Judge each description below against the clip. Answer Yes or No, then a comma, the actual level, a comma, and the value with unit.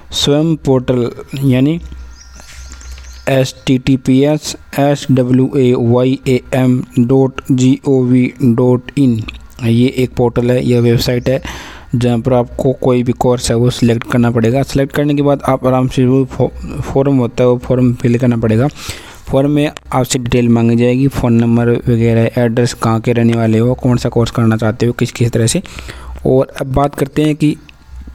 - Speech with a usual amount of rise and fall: No, narrow, 2.2 semitones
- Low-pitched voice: Yes, low, 125 Hz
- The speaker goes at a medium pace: Yes, average, 175 wpm